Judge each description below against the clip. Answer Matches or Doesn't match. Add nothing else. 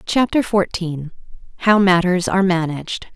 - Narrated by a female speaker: Matches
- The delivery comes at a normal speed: Doesn't match